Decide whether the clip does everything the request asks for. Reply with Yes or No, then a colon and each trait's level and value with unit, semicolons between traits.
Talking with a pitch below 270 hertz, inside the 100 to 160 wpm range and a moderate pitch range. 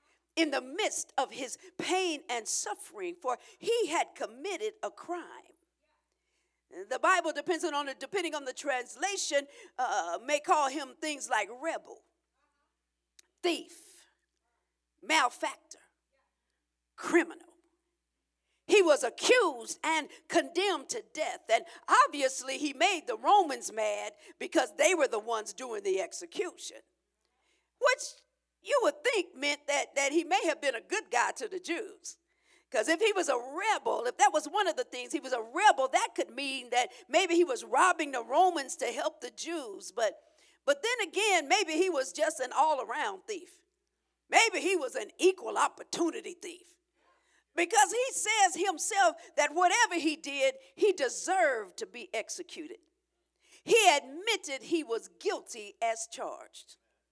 No: very high, 345 Hz; average, 150 wpm; average, 4.9 semitones